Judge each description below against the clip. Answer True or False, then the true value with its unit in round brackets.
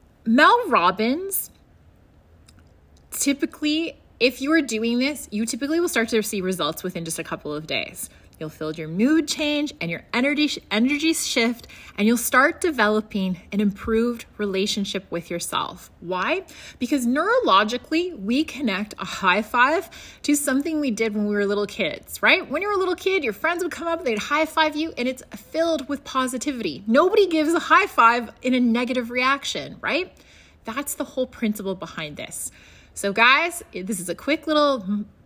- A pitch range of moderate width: False (6.7 semitones)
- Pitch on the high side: True (245 Hz)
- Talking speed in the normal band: True (170 wpm)